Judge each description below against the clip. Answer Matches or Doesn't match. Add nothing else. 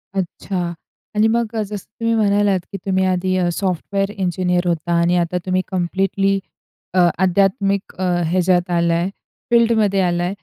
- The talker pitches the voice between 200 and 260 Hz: Doesn't match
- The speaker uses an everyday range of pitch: Doesn't match